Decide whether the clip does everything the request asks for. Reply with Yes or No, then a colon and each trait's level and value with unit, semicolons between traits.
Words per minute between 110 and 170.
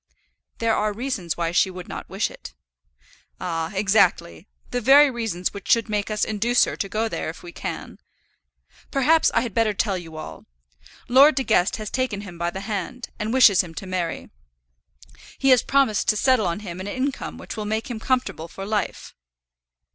No: average, 190 wpm